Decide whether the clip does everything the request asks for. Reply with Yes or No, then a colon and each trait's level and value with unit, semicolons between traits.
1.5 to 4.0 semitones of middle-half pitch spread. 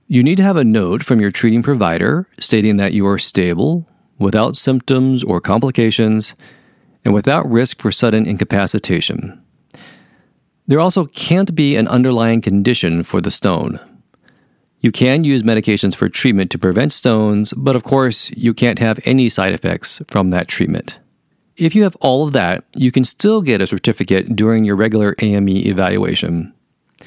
No: average, 4.6 semitones